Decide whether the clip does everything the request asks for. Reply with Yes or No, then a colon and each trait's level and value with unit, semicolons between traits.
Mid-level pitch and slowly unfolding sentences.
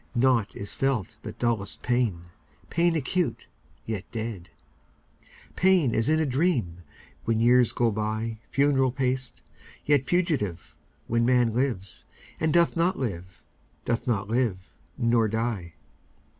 No: low, 120 Hz; slow, 100 wpm